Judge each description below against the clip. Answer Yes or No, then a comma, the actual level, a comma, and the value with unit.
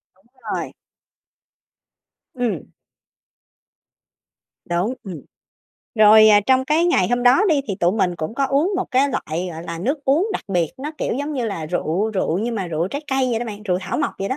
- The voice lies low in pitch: No, high, 220 Hz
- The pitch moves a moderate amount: No, wide, 6.8 semitones